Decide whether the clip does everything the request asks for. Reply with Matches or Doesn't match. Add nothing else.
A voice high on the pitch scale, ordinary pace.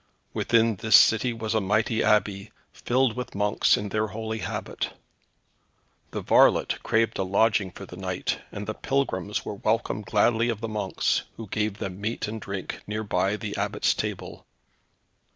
Doesn't match